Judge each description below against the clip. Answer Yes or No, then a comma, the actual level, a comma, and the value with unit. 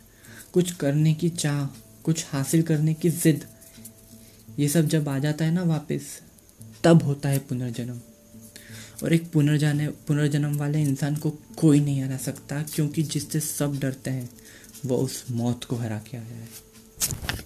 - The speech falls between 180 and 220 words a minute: No, average, 155 wpm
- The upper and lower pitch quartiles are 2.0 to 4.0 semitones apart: No, average, 4.9 semitones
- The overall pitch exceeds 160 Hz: No, medium, 140 Hz